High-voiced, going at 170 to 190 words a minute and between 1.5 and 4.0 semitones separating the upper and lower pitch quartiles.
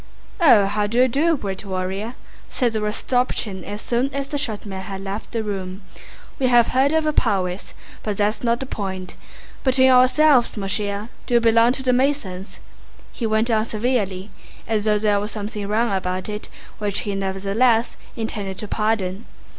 Yes: high, 215 Hz; average, 180 wpm; average, 3.7 semitones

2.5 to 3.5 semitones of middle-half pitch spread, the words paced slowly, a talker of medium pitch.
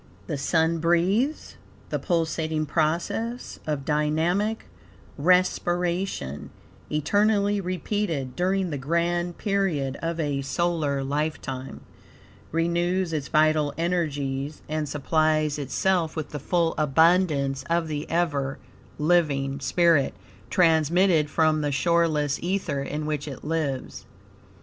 Yes: average, 3.1 semitones; slow, 105 wpm; medium, 160 Hz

